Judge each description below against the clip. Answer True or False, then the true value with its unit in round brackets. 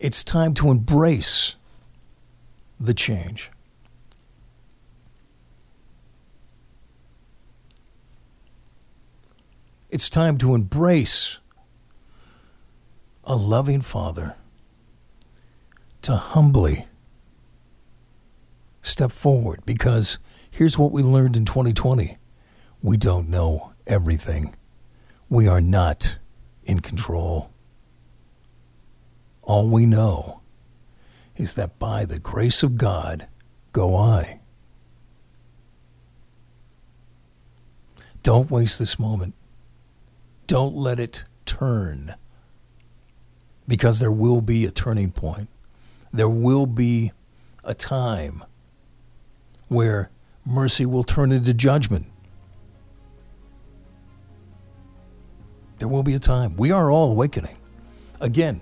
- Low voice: True (105 Hz)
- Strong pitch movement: True (8.4 semitones)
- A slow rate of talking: True (85 wpm)